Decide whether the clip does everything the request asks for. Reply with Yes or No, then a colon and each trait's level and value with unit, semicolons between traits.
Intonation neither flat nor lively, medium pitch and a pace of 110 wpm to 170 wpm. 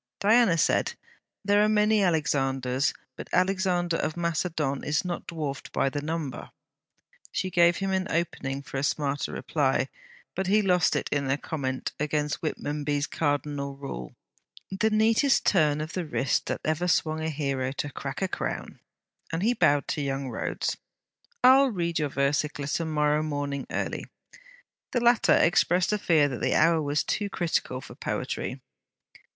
Yes: average, 4.3 semitones; medium, 155 Hz; average, 160 wpm